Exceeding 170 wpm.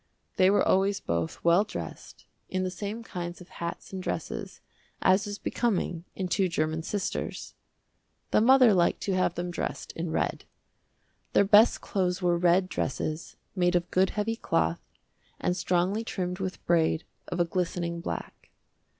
No: average, 160 wpm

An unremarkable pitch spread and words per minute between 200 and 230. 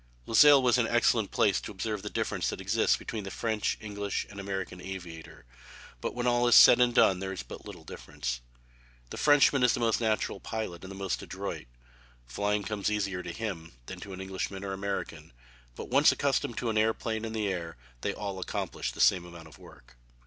Yes: average, 3.2 semitones; fast, 205 wpm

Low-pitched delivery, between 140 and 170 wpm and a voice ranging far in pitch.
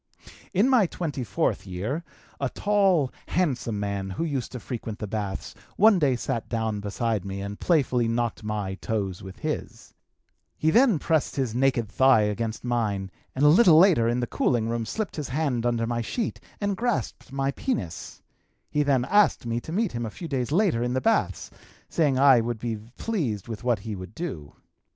No: low, 120 Hz; average, 190 wpm; wide, 6.2 semitones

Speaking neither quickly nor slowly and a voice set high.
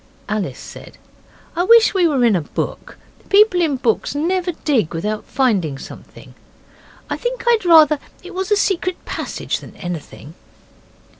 Yes: average, 150 wpm; very high, 310 Hz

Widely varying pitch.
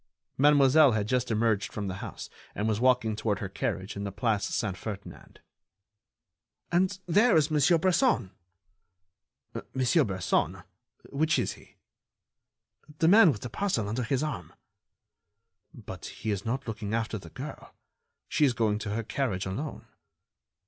Yes: wide, 6.0 semitones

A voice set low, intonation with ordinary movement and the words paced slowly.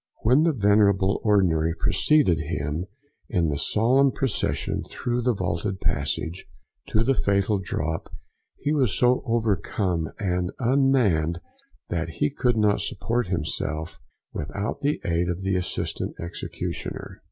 No: low, 100 Hz; wide, 6.2 semitones; slow, 130 wpm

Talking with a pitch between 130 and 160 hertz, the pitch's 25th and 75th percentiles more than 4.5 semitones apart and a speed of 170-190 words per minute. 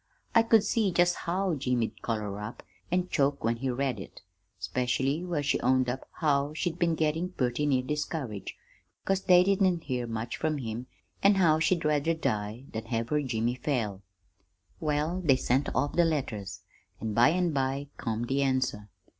Yes: medium, 140 Hz; wide, 5.5 semitones; average, 175 wpm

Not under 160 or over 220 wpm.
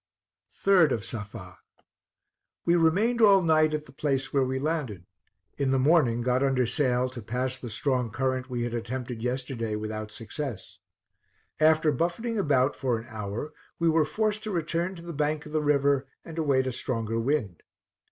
Yes: average, 170 wpm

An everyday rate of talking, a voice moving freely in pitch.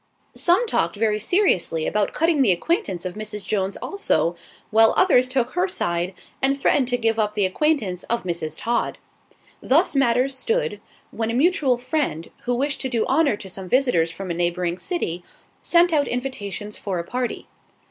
Yes: average, 175 wpm; wide, 6.8 semitones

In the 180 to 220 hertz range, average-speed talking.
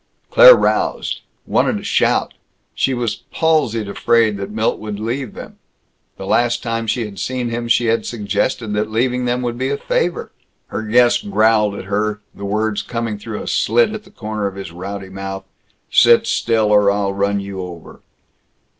No: low, 110 Hz; average, 180 wpm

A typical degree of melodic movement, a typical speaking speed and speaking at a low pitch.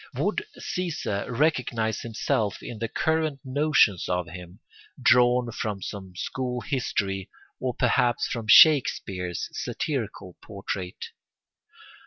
No: average, 5.0 semitones; slow, 105 wpm; low, 115 Hz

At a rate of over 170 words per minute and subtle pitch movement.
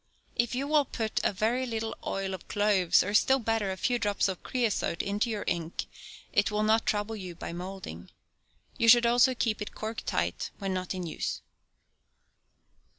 No: average, 180 wpm; average, 3.6 semitones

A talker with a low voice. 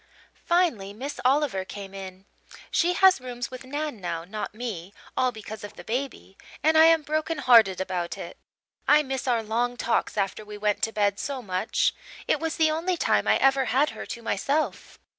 No: high, 240 Hz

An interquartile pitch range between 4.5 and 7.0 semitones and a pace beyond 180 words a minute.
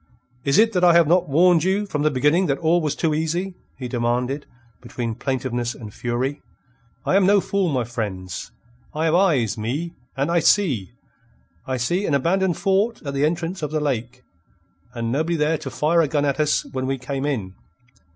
Yes: average, 5.3 semitones; average, 195 wpm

